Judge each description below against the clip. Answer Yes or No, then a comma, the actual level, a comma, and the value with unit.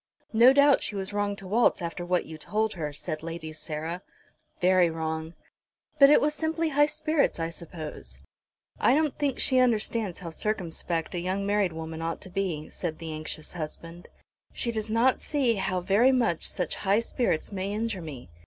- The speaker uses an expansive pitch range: Yes, wide, 5.9 semitones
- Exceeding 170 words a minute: Yes, average, 180 wpm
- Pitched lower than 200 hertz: Yes, high, 190 Hz